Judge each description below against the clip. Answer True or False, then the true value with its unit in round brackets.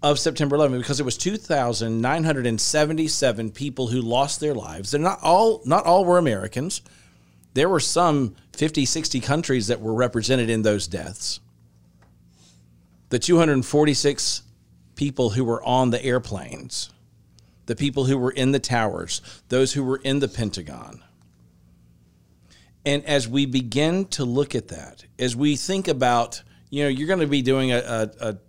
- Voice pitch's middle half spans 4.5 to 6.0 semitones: True (5.6 semitones)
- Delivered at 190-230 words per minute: False (155 wpm)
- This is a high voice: False (125 Hz)